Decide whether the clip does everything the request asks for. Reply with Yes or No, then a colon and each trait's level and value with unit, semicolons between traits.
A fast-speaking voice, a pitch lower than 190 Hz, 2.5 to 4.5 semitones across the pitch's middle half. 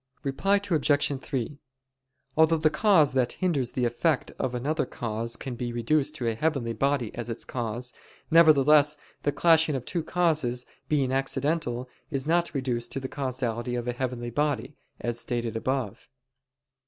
No: average, 155 wpm; low, 135 Hz; average, 4.0 semitones